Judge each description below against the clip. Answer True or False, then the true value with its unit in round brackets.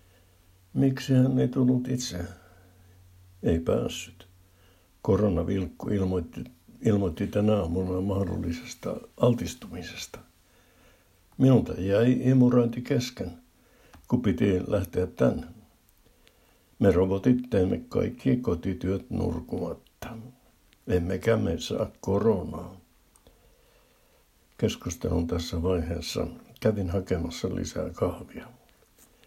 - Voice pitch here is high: False (95 Hz)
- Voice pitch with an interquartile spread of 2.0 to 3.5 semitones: False (4.1 semitones)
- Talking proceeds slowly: True (80 wpm)